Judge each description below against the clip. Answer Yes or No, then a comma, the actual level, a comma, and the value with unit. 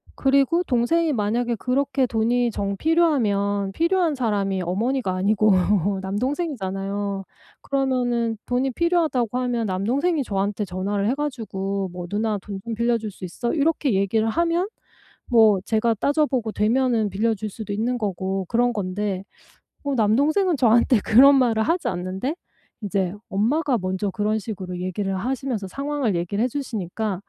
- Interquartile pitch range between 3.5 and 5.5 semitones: Yes, average, 5.1 semitones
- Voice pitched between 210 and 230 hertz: Yes, high, 225 Hz